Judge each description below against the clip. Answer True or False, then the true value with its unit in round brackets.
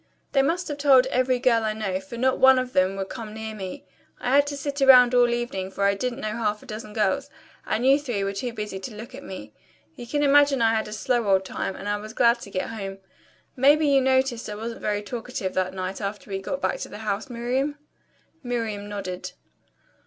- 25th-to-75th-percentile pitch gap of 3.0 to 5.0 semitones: True (4.3 semitones)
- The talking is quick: True (230 wpm)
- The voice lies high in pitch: True (230 Hz)